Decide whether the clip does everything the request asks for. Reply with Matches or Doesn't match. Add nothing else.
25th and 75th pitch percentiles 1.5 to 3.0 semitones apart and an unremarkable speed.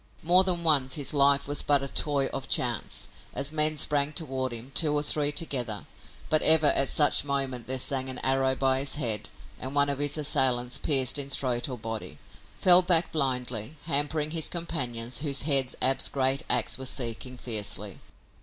Matches